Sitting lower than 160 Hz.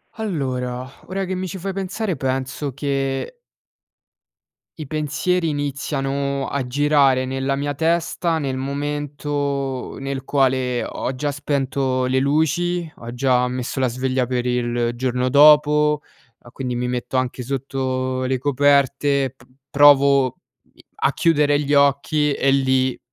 Yes: medium, 140 Hz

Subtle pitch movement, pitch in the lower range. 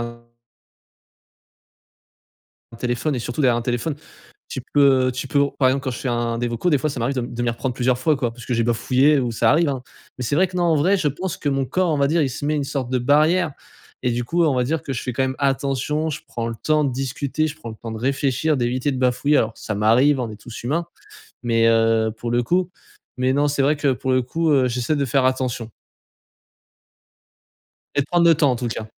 No: average, 3.5 semitones; low, 130 Hz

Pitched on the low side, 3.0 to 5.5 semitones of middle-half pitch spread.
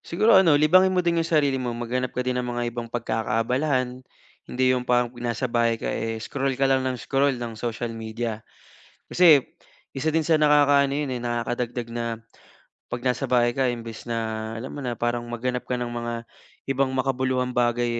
No: low, 125 Hz; narrow, 2.4 semitones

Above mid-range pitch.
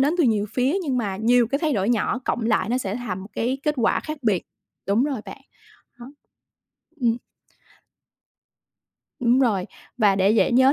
Yes: high, 235 Hz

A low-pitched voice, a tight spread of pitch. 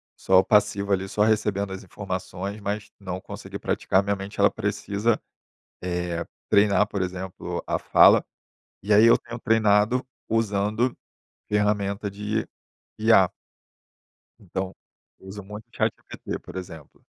Yes: low, 100 Hz; narrow, 1.8 semitones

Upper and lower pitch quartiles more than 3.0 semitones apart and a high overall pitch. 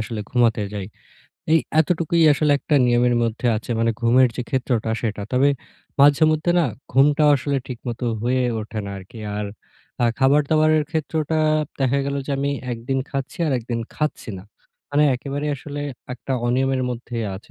No: average, 3.5 semitones; low, 135 Hz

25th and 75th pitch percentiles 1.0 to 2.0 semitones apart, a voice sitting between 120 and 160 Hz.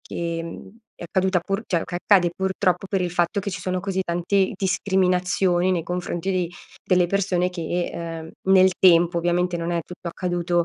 No: narrow, 1.6 semitones; medium, 180 Hz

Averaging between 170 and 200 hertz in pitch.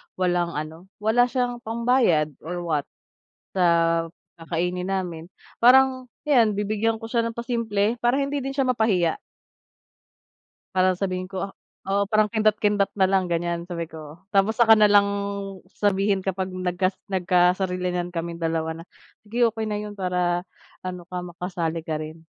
Yes: high, 190 Hz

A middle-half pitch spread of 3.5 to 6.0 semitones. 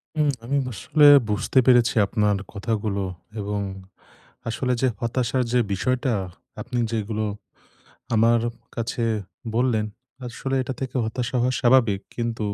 No: average, 3.0 semitones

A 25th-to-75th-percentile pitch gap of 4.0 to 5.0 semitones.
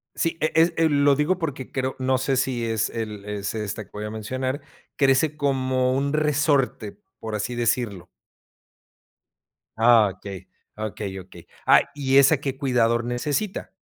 Yes: average, 4.5 semitones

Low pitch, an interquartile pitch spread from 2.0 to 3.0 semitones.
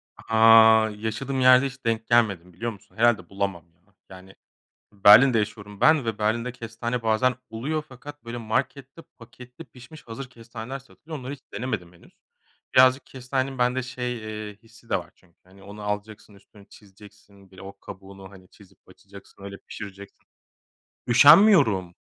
No: low, 110 Hz; average, 4.1 semitones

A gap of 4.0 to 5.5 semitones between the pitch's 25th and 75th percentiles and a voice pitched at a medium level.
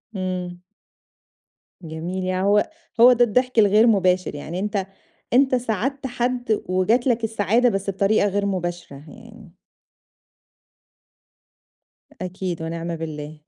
No: average, 4.5 semitones; high, 195 Hz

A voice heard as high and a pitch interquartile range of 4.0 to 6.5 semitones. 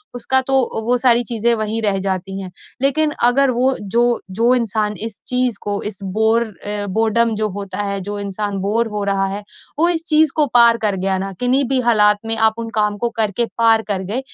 No: high, 220 Hz; average, 3.1 semitones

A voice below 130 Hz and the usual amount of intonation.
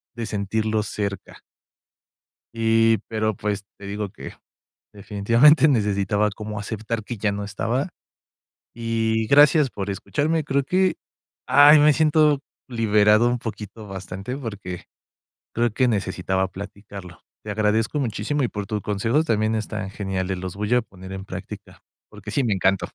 Yes: low, 110 Hz; average, 3.1 semitones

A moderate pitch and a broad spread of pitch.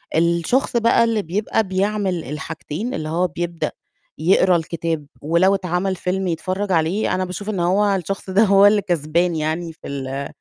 No: medium, 180 Hz; average, 3.2 semitones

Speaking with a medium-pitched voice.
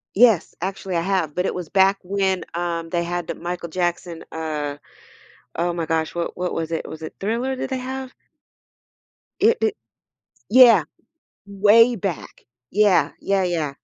Yes: medium, 180 Hz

